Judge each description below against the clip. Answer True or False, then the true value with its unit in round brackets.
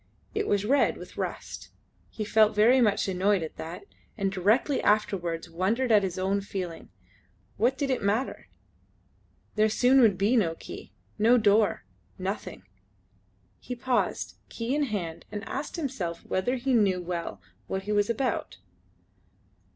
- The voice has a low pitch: False (210 Hz)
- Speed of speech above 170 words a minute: False (150 wpm)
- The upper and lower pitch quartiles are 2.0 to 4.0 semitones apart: False (4.5 semitones)